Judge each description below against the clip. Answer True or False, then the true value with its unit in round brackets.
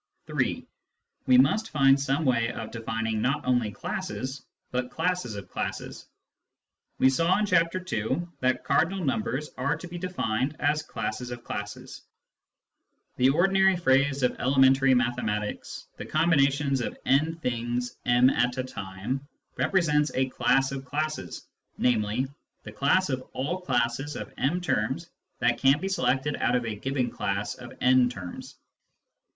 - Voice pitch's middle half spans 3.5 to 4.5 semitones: True (4.0 semitones)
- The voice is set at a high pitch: False (135 Hz)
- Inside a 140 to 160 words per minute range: True (150 wpm)